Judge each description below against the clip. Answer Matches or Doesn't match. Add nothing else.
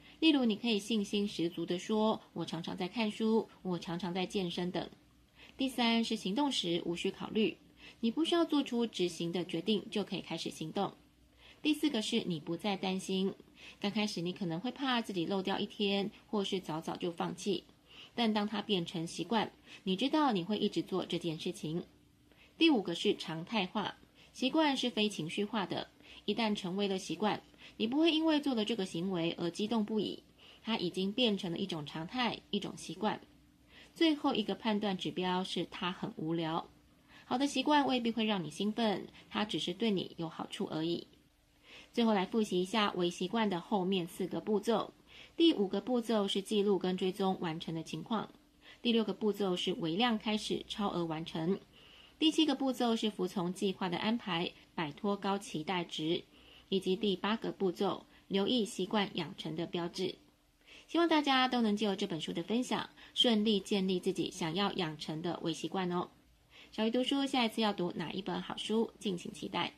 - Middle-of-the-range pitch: Doesn't match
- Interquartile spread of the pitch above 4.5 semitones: Doesn't match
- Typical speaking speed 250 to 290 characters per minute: Matches